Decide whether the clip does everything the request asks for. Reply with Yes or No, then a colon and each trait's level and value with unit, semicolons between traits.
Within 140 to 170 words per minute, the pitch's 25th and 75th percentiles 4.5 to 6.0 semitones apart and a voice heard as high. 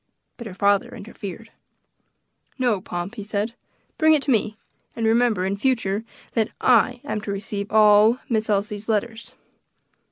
No: average, 150 wpm; narrow, 2.6 semitones; high, 215 Hz